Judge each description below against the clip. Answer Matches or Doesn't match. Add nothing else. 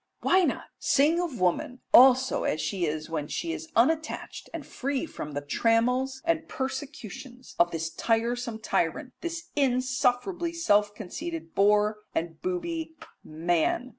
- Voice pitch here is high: Matches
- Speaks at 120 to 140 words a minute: Matches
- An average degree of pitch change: Doesn't match